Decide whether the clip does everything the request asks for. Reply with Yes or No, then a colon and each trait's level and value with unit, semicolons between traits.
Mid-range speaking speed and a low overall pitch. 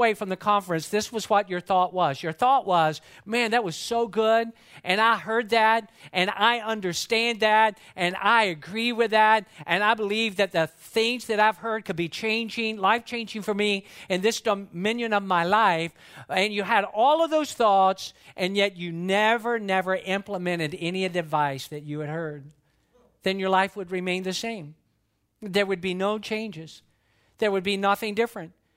No: average, 185 wpm; high, 200 Hz